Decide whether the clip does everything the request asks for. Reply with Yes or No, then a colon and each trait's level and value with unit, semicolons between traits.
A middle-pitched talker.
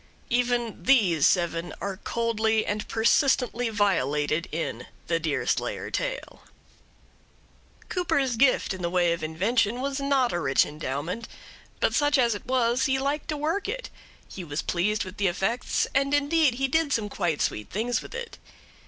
No: high, 225 Hz